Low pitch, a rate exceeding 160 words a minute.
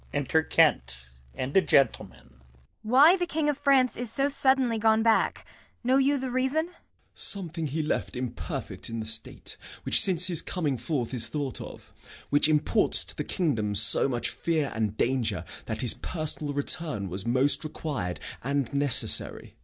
No: medium, 150 Hz; average, 170 wpm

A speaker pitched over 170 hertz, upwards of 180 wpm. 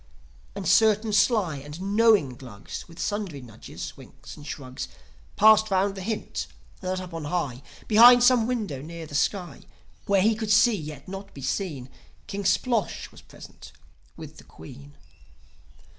No: high, 190 Hz; average, 155 wpm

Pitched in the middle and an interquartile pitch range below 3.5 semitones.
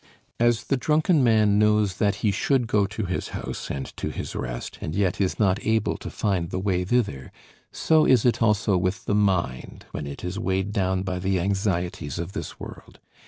No: low, 100 Hz; average, 3.0 semitones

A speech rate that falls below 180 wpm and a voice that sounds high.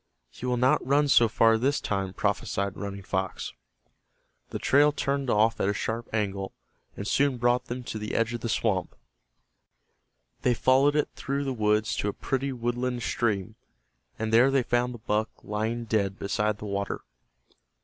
No: average, 170 wpm; low, 115 Hz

